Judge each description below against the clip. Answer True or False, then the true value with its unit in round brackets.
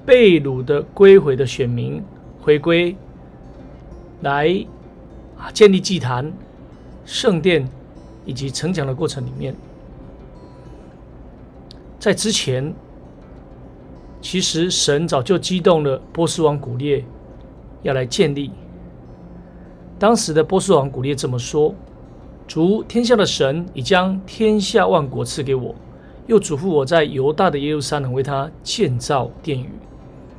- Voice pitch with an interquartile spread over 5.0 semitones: True (5.5 semitones)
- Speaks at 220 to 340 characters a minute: False (180 characters per minute)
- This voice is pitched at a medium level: True (145 Hz)